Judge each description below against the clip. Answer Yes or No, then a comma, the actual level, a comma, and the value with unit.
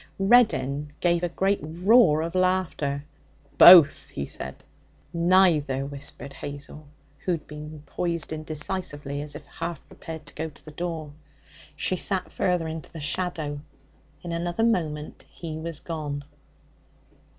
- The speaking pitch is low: No, medium, 160 Hz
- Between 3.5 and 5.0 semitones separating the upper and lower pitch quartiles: No, average, 3.1 semitones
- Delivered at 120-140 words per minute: Yes, slow, 135 wpm